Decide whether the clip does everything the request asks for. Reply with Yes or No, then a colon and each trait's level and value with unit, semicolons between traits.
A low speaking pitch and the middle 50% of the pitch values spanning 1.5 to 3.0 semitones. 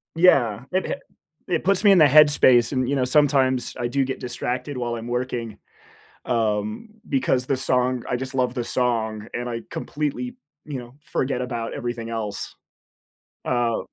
Yes: low, 125 Hz; narrow, 2.4 semitones